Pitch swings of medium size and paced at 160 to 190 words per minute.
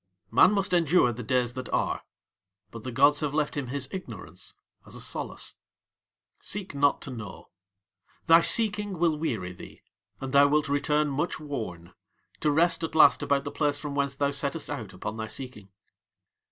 Yes: average, 3.8 semitones; average, 175 wpm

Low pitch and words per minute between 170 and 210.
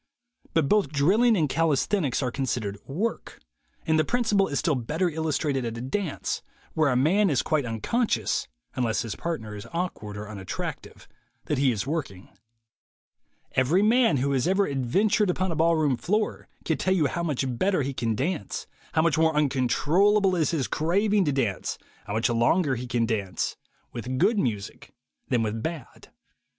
No: medium, 145 Hz; average, 175 wpm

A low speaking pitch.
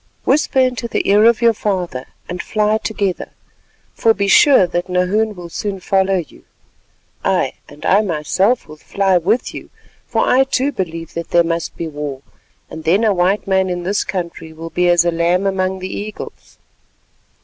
No: high, 190 Hz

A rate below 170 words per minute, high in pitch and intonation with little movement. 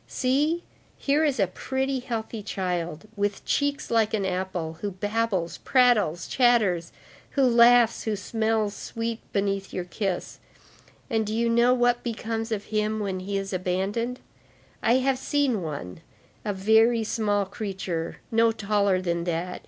No: average, 145 wpm; high, 215 Hz; average, 3.8 semitones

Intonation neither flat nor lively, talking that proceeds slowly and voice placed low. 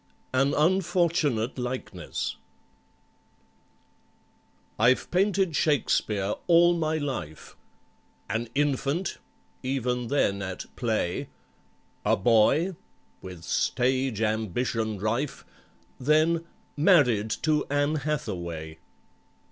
No: wide, 6.1 semitones; slow, 80 wpm; low, 130 Hz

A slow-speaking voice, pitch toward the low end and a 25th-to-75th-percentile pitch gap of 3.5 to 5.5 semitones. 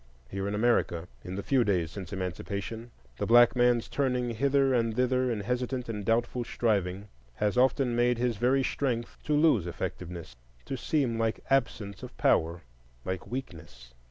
No: average, 160 wpm; low, 115 Hz; average, 4.2 semitones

